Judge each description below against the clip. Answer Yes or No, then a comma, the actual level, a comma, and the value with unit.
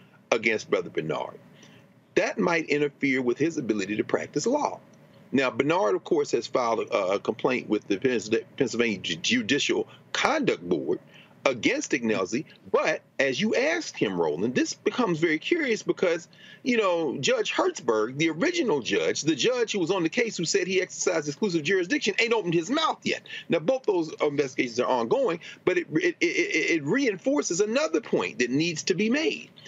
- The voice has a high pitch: Yes, high, 230 Hz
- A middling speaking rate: Yes, average, 170 wpm